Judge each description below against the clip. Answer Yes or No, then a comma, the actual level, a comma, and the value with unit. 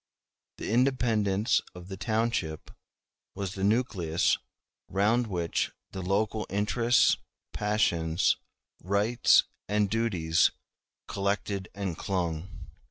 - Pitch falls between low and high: No, low, 100 Hz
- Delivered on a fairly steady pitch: No, average, 3.4 semitones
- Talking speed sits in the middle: No, slow, 95 wpm